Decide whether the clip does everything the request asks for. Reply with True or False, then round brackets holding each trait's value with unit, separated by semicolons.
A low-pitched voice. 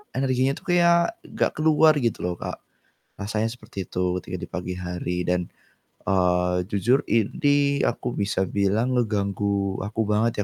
True (105 Hz)